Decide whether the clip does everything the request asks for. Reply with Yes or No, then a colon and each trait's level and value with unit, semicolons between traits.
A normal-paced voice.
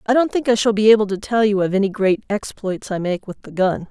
No: fast, 290 wpm